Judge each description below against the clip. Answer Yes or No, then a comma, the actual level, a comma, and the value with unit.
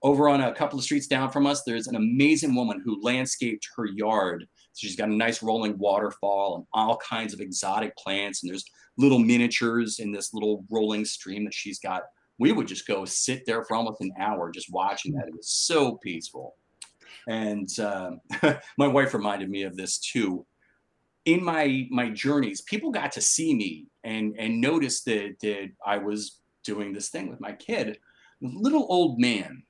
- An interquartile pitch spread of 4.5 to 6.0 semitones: Yes, wide, 5.4 semitones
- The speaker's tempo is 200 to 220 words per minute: No, average, 185 wpm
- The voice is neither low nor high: No, low, 115 Hz